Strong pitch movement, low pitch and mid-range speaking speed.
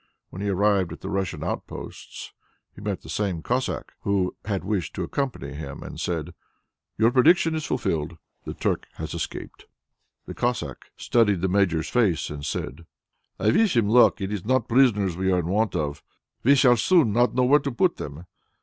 Yes: wide, 5.7 semitones; low, 100 Hz; average, 185 wpm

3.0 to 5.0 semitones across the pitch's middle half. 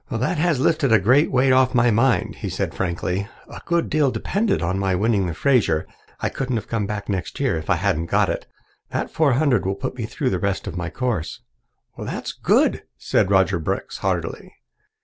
No: wide, 5.6 semitones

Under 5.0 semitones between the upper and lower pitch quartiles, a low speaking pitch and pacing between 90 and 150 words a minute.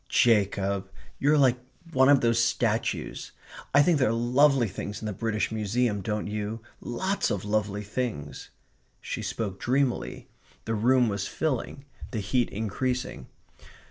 Yes: average, 3.8 semitones; low, 115 Hz; average, 145 wpm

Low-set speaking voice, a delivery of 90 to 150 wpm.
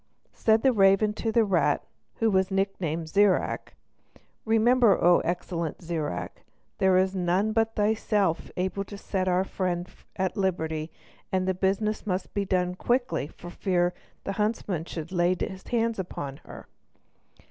No: high, 190 Hz; average, 145 wpm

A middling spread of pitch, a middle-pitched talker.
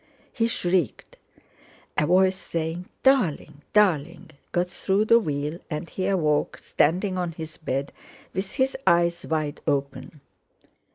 Yes: average, 3.8 semitones; medium, 170 Hz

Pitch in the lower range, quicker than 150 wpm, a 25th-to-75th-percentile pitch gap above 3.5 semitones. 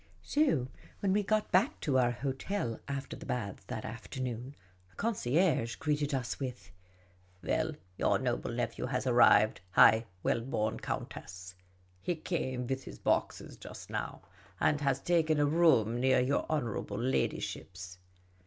No: low, 130 Hz; average, 145 wpm; average, 5.1 semitones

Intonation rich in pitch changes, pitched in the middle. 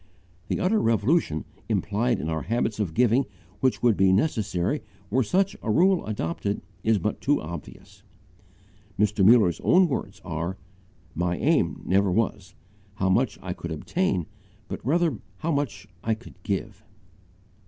No: wide, 6.0 semitones; low, 105 Hz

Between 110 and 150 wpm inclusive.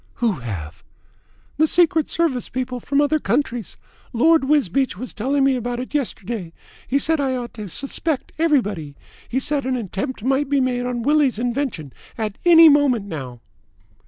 No: average, 170 wpm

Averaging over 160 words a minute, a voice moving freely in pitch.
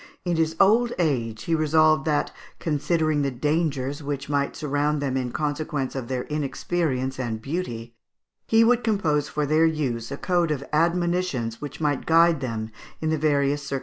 No: average, 180 wpm; average, 3.3 semitones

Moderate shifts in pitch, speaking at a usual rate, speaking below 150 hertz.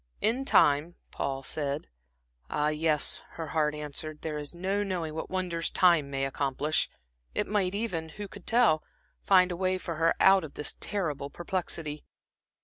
No: average, 3.8 semitones; average, 160 wpm; medium, 160 Hz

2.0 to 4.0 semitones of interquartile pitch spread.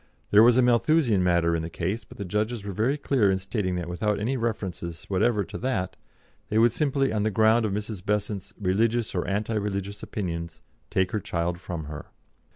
Yes: average, 3.7 semitones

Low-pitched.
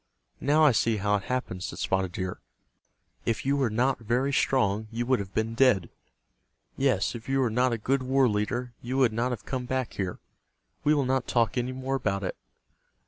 Yes: low, 125 Hz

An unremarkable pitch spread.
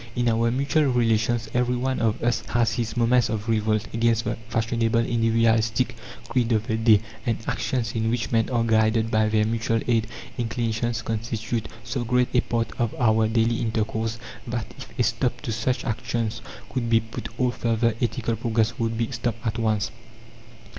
No: narrow, 1.2 semitones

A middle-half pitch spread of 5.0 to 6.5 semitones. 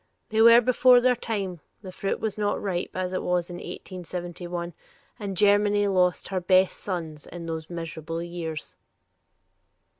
No: average, 3.0 semitones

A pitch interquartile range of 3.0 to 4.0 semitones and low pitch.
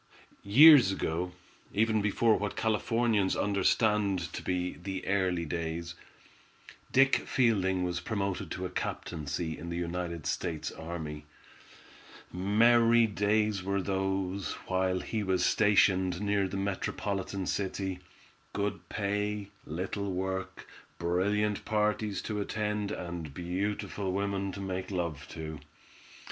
No: narrow, 2.5 semitones; very low, 95 Hz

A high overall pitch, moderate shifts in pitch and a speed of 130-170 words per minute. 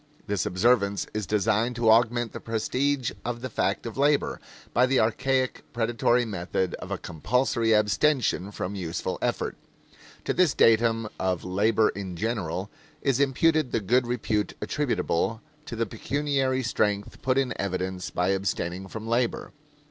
No: low, 115 Hz; average, 3.9 semitones; average, 150 wpm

